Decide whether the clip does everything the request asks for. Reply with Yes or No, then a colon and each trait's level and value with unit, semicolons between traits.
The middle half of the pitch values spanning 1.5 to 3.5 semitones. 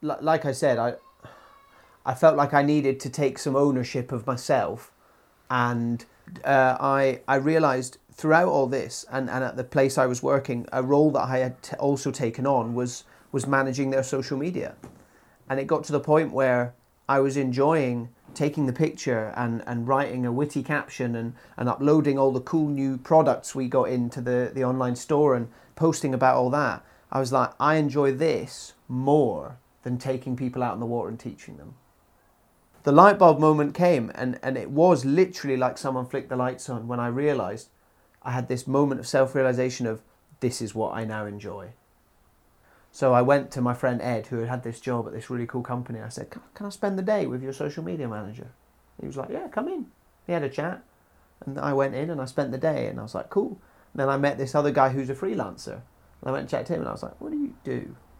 Yes: narrow, 2.5 semitones